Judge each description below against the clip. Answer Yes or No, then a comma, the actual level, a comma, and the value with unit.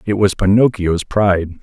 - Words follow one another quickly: No, average, 150 wpm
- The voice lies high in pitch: No, low, 100 Hz